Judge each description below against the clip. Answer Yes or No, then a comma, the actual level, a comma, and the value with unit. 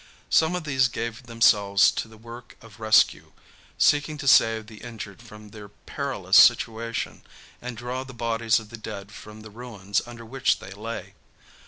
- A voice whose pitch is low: Yes, low, 115 Hz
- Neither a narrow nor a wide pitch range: No, narrow, 2.2 semitones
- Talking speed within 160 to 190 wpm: Yes, average, 170 wpm